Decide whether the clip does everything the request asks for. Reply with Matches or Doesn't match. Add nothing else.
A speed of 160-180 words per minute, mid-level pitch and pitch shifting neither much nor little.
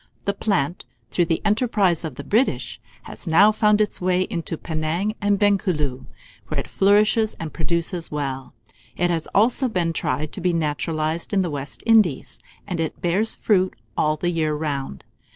Matches